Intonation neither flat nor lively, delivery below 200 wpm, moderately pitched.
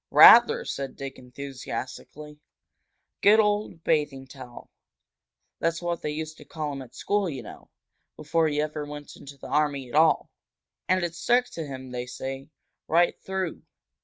Yes: average, 3.8 semitones; average, 160 wpm; medium, 150 Hz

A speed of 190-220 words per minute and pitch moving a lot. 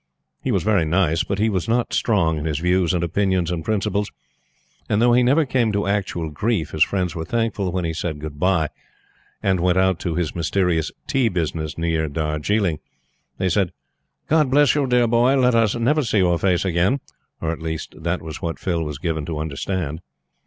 No: average, 200 wpm; average, 4.9 semitones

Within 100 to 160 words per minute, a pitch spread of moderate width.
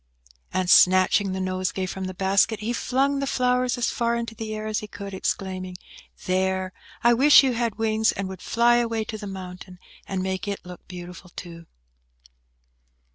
No: average, 180 wpm; average, 3.8 semitones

